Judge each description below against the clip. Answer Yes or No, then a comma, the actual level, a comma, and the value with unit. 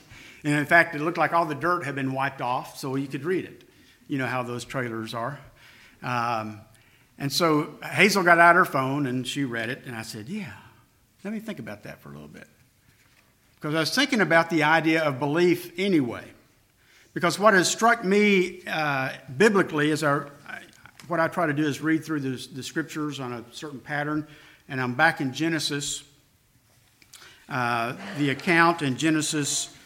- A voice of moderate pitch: Yes, medium, 150 Hz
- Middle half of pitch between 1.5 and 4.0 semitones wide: No, average, 4.4 semitones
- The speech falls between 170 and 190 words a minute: Yes, average, 185 wpm